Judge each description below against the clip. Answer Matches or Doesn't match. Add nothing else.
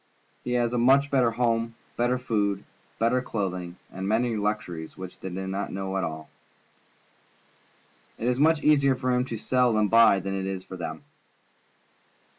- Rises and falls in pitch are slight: Doesn't match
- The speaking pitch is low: Matches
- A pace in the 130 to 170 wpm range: Matches